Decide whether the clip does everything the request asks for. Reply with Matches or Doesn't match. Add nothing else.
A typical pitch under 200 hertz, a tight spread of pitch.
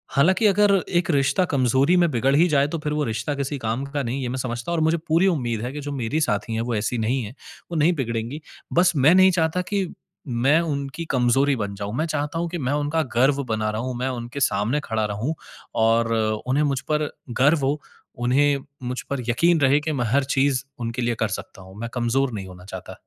Doesn't match